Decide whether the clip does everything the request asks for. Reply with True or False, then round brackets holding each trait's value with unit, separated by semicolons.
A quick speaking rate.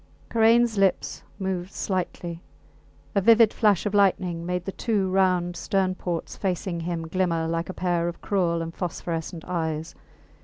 False (150 wpm)